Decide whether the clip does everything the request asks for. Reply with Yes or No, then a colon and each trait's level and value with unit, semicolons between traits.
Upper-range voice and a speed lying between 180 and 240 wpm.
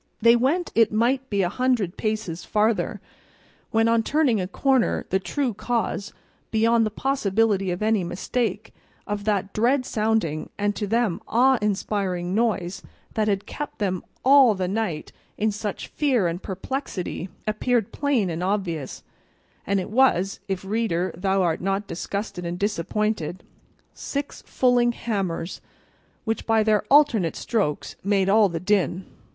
No: high, 210 Hz; average, 145 wpm